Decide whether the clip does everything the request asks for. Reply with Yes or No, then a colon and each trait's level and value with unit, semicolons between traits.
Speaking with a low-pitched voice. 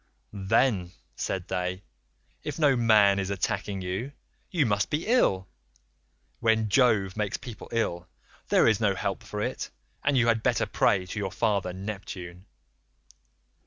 Yes: low, 100 Hz